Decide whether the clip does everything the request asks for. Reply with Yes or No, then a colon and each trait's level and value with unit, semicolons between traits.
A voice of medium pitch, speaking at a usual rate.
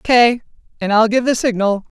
No: high, 225 Hz; average, 180 wpm